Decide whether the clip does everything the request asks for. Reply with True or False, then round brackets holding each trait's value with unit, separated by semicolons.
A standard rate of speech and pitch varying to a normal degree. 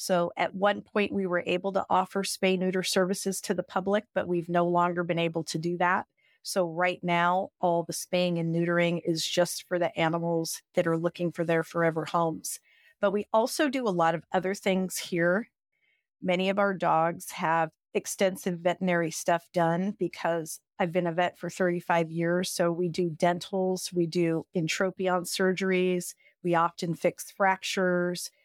False (175 wpm; 1.8 semitones)